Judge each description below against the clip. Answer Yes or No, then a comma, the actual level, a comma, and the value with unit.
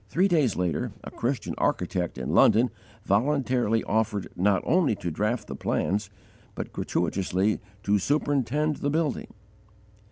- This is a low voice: Yes, low, 110 Hz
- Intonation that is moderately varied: No, wide, 6.7 semitones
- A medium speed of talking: No, slow, 130 wpm